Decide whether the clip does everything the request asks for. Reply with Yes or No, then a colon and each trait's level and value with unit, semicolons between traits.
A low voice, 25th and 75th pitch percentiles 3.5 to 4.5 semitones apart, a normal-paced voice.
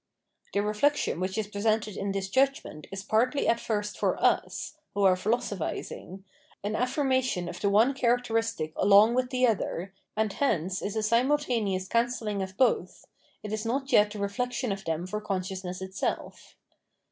No: high, 210 Hz; average, 3.9 semitones; average, 160 wpm